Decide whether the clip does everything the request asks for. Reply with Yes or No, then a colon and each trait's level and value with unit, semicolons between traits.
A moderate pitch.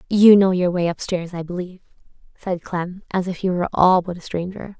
Yes: medium, 180 Hz